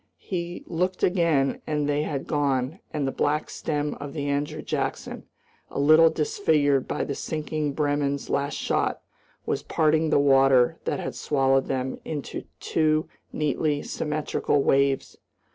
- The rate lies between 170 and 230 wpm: No, average, 145 wpm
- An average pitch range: No, narrow, 2.0 semitones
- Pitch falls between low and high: Yes, medium, 145 Hz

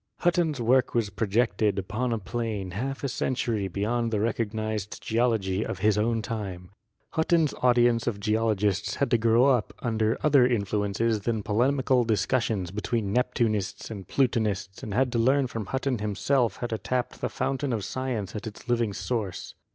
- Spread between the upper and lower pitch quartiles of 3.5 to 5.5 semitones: No, average, 3.1 semitones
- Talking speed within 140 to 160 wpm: No, average, 175 wpm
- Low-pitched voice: Yes, low, 115 Hz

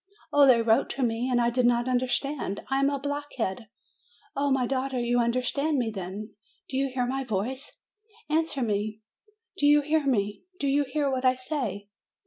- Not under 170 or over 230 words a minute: Yes, average, 185 wpm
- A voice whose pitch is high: Yes, very high, 255 Hz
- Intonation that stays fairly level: No, average, 3.1 semitones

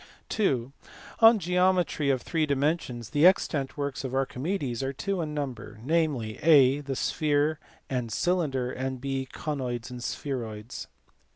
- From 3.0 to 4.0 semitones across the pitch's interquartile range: Yes, average, 3.7 semitones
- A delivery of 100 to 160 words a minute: Yes, slow, 135 wpm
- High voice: No, medium, 140 Hz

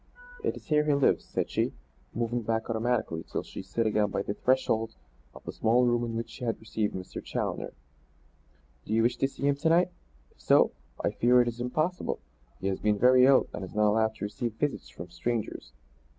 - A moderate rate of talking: No, fast, 210 wpm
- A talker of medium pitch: No, low, 115 Hz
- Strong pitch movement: No, average, 2.9 semitones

